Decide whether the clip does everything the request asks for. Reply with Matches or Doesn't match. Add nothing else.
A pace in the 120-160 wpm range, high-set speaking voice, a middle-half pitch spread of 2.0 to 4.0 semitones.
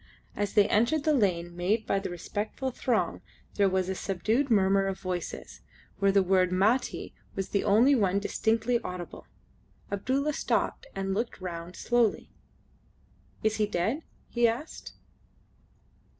Matches